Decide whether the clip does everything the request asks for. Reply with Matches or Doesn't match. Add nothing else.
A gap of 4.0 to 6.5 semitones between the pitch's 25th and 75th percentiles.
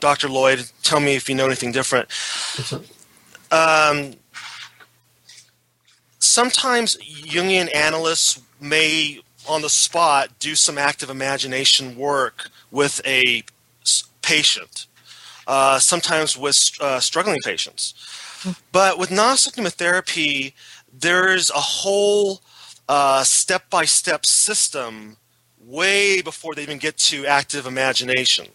Matches